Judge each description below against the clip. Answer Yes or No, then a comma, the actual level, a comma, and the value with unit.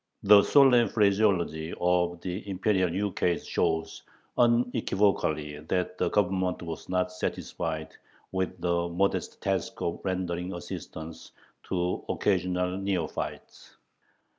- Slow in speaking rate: Yes, slow, 105 wpm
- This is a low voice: Yes, very low, 90 Hz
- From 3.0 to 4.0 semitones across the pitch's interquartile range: No, narrow, 2.4 semitones